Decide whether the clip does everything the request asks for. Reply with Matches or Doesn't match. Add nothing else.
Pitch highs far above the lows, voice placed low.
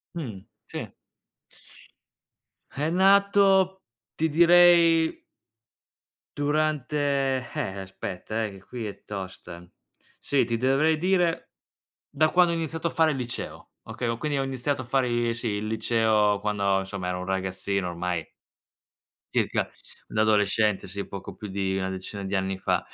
Matches